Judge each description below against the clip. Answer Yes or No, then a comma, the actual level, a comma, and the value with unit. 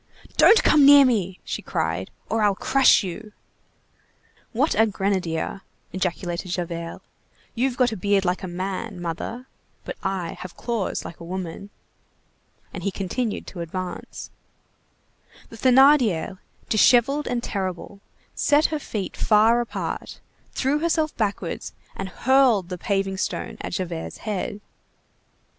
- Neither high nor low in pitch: No, high, 200 Hz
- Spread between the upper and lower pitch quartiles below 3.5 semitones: No, average, 4.9 semitones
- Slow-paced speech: Yes, slow, 130 wpm